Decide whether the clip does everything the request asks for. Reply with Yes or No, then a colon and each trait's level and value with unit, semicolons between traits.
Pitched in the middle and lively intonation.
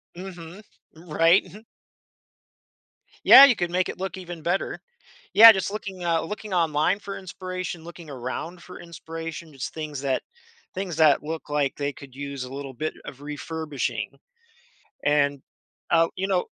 No: medium, 165 Hz; average, 3.8 semitones